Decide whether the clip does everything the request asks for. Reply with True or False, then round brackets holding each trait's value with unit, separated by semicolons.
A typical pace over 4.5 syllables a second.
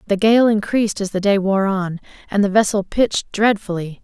True (5.4 syllables/s)